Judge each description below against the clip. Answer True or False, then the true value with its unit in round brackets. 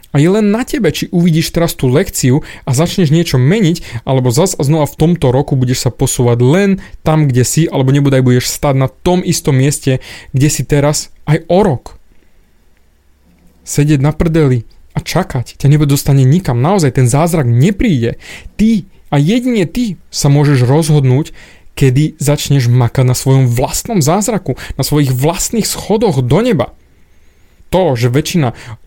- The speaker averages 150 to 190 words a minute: True (165 wpm)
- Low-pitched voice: False (145 Hz)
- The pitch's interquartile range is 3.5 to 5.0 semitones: True (4.5 semitones)